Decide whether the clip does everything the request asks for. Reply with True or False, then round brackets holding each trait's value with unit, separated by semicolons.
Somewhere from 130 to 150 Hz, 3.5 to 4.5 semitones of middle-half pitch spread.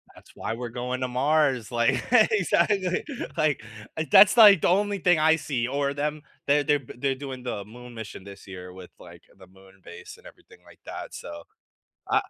False (135 Hz; 5.2 semitones)